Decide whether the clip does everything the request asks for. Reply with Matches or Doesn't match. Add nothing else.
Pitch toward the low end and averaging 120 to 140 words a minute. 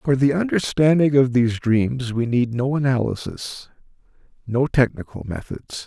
Matches